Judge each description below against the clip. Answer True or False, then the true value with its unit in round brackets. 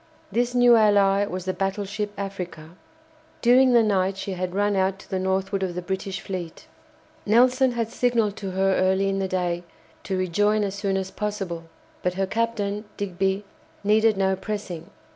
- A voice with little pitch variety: True (1.9 semitones)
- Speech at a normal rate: True (170 wpm)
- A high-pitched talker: True (195 Hz)